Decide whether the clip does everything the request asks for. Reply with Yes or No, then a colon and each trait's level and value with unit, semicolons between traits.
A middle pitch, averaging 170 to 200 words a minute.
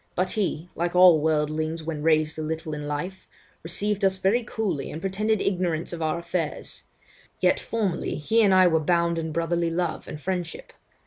Yes: medium, 170 Hz; average, 180 wpm